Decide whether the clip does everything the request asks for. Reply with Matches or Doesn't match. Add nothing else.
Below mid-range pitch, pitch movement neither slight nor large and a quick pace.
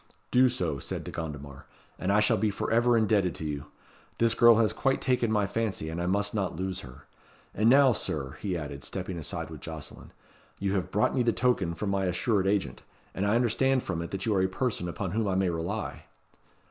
Matches